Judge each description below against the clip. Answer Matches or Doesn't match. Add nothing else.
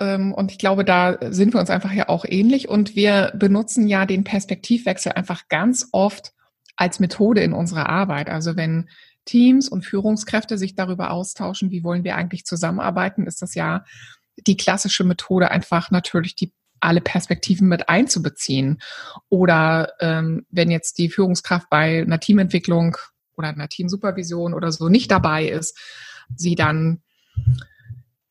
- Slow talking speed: Doesn't match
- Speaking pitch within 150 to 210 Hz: Matches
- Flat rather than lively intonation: Doesn't match